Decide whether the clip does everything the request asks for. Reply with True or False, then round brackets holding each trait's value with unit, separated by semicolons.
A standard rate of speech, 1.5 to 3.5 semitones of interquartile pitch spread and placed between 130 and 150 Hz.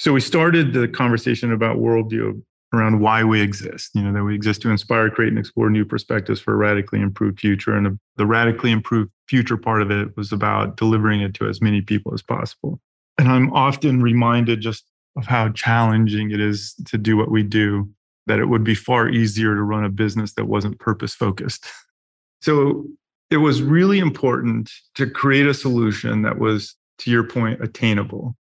False (190 wpm; 2.4 semitones; 110 Hz)